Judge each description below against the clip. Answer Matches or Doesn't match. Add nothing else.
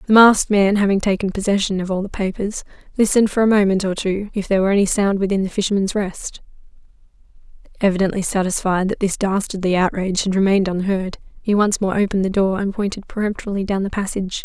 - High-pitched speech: Matches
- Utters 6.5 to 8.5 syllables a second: Matches